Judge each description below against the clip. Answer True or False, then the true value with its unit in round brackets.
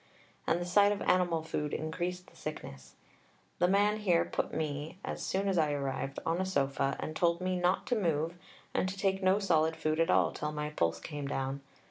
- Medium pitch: True (165 Hz)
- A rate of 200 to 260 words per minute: True (205 wpm)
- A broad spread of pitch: False (3.8 semitones)